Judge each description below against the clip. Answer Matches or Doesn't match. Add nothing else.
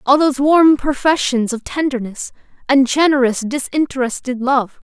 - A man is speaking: Doesn't match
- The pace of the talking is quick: Doesn't match